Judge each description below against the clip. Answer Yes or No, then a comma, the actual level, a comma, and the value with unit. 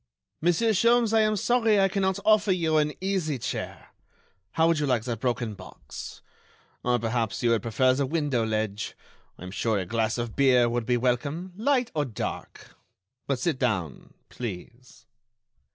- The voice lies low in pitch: Yes, low, 130 Hz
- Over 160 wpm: Yes, average, 170 wpm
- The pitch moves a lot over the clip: Yes, wide, 7.9 semitones